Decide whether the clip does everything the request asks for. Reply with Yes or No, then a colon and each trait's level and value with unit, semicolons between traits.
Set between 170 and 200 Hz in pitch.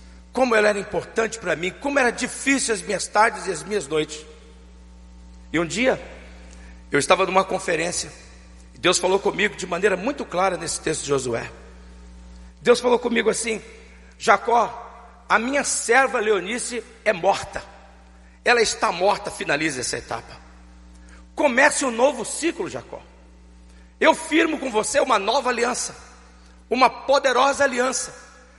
Yes: high, 190 Hz